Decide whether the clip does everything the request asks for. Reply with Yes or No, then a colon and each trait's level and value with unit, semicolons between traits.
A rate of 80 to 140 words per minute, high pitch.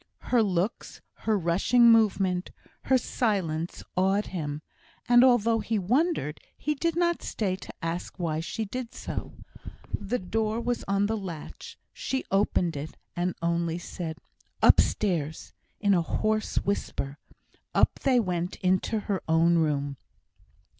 Yes: slow, 135 wpm; high, 195 Hz